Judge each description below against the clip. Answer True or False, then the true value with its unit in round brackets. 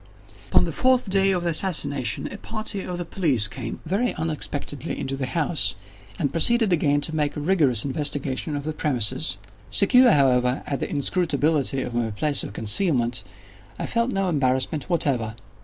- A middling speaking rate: True (165 wpm)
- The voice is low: False (145 Hz)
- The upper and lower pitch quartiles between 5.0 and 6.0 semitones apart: True (5.5 semitones)